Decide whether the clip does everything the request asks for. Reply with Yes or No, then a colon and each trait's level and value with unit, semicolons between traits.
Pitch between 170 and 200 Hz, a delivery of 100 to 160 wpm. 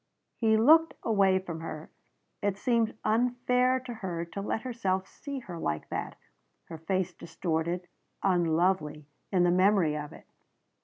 Yes: high, 190 Hz; average, 145 wpm